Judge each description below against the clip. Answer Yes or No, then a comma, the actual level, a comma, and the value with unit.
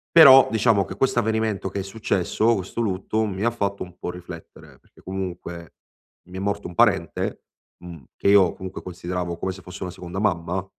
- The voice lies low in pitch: Yes, very low, 95 Hz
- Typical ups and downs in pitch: Yes, average, 3.2 semitones